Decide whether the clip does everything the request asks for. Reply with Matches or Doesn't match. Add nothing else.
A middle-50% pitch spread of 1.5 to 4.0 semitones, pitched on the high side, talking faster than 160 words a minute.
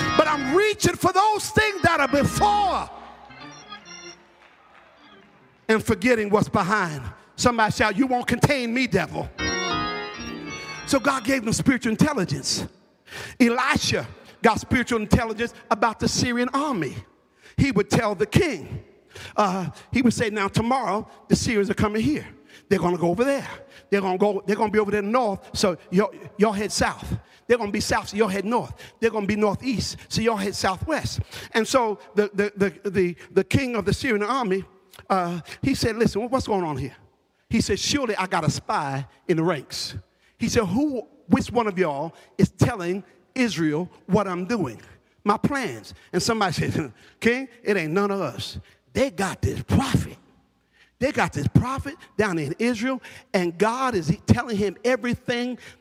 Doesn't match